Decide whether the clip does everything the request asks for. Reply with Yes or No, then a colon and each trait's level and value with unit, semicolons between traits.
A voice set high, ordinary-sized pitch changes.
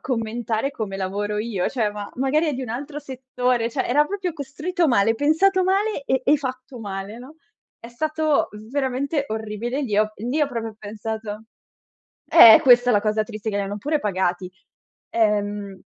Yes: high, 240 Hz; average, 5.0 semitones